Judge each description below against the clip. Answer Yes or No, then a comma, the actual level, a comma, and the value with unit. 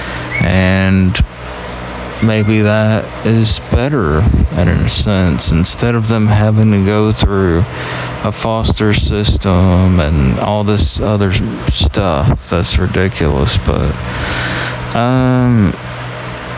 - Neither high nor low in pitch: No, very low, 95 Hz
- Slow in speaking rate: Yes, slow, 100 wpm